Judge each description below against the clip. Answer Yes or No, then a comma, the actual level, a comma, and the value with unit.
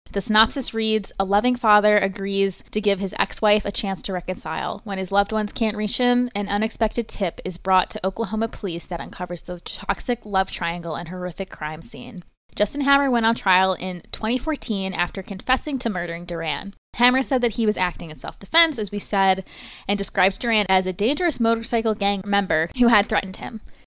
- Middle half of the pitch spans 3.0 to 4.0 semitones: Yes, average, 3.3 semitones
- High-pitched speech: Yes, high, 200 Hz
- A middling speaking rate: Yes, average, 195 wpm